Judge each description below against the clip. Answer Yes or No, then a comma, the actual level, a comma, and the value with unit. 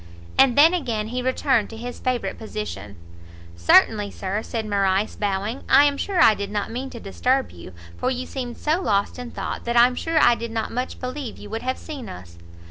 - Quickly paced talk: Yes, fast, 210 wpm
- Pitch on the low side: No, high, 235 Hz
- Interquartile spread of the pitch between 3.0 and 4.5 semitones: Yes, average, 3.9 semitones